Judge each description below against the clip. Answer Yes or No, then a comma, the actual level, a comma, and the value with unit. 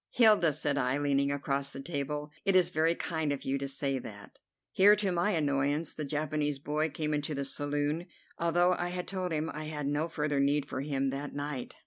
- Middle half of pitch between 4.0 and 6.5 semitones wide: No, average, 2.7 semitones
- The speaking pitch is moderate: Yes, medium, 150 Hz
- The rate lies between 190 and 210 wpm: Yes, fast, 205 wpm